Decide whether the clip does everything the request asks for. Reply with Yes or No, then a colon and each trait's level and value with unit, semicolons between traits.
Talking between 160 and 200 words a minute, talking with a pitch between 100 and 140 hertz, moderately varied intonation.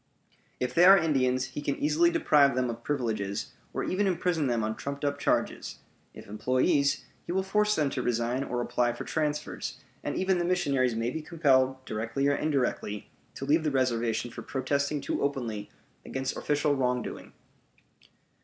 Yes: average, 170 wpm; low, 135 Hz; average, 3.6 semitones